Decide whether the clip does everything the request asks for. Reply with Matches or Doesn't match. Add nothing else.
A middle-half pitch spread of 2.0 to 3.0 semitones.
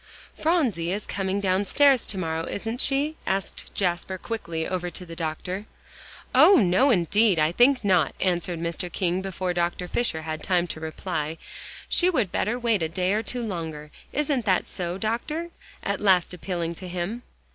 Doesn't match